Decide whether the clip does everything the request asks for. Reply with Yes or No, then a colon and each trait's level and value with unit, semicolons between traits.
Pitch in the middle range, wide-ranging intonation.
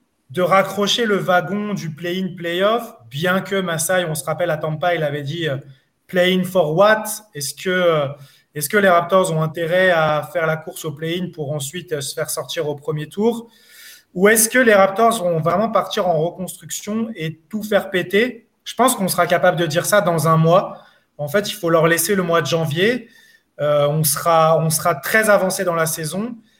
No: medium, 180 Hz; average, 4.3 semitones